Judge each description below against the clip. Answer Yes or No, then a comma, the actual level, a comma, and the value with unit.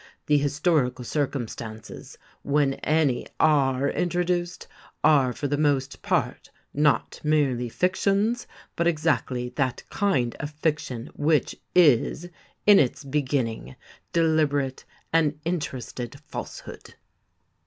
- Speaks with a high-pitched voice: No, medium, 145 Hz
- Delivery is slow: Yes, slow, 100 wpm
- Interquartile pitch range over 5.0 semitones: No, average, 3.6 semitones